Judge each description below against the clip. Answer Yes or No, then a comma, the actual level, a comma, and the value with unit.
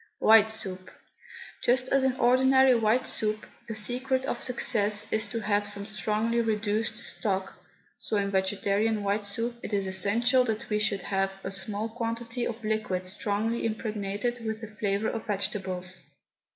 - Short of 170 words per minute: Yes, average, 155 wpm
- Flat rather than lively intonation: Yes, narrow, 2.3 semitones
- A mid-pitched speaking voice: No, high, 215 Hz